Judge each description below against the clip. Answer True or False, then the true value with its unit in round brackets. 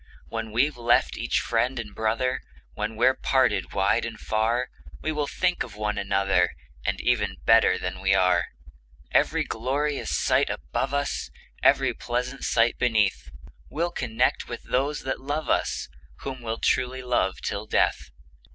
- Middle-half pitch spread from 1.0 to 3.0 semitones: False (3.8 semitones)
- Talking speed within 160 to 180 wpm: False (150 wpm)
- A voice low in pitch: True (120 Hz)